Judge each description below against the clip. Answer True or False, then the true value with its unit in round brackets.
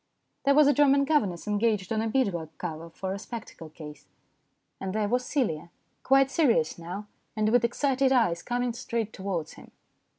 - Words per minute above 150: True (175 wpm)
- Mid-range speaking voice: False (220 Hz)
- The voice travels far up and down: True (6.5 semitones)